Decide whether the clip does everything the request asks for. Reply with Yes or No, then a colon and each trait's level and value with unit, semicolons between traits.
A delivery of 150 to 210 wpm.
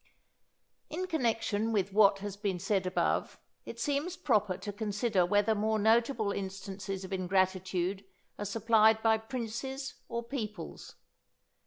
No: slow, 135 wpm